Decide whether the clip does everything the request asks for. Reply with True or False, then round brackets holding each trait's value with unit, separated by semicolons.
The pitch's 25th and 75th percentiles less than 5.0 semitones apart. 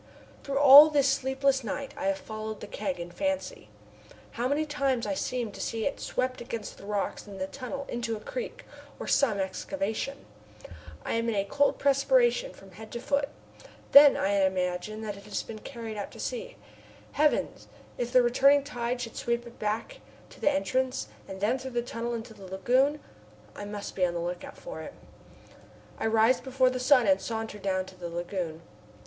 False (5.3 semitones)